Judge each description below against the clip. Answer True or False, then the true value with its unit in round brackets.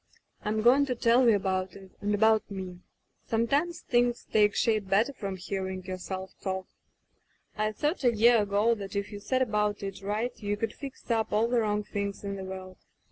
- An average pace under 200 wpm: False (205 wpm)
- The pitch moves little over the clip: False (3.0 semitones)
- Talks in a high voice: True (210 Hz)